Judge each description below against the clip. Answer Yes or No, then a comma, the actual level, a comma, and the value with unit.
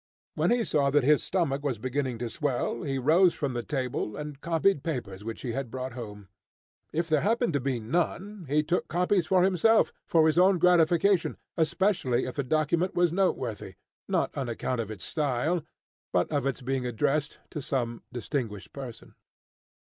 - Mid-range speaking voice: Yes, medium, 145 Hz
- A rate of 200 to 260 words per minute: No, average, 180 wpm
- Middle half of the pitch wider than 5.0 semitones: Yes, wide, 5.5 semitones